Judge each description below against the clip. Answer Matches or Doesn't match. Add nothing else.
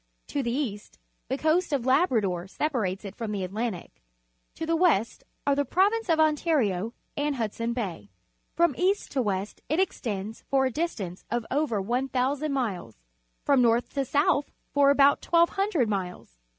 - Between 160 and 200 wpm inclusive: Matches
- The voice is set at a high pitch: Matches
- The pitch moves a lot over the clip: Matches